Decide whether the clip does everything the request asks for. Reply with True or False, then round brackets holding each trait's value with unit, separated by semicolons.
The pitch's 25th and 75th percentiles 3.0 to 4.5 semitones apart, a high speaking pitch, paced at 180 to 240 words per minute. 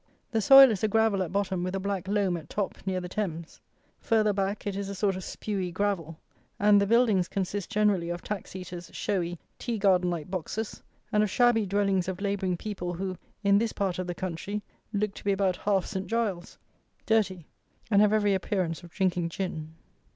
False (2.5 semitones; 195 Hz; 200 wpm)